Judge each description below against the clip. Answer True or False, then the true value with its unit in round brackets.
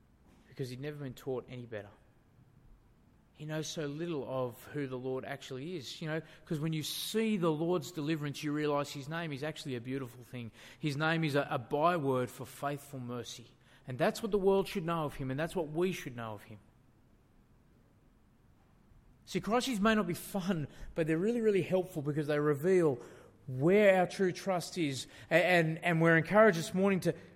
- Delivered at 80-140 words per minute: False (195 wpm)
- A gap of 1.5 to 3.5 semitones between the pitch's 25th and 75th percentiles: False (5.0 semitones)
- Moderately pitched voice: True (155 Hz)